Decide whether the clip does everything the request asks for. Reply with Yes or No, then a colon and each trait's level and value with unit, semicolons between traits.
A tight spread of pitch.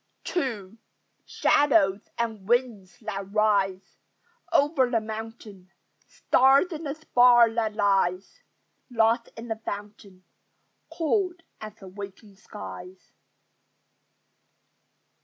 No: average, 3.8 semitones